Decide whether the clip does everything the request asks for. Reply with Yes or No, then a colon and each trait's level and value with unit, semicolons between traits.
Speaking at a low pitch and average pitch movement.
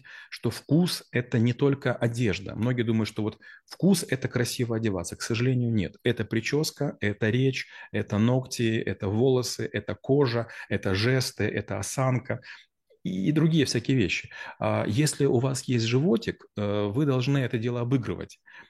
Yes: low, 120 Hz; average, 3.5 semitones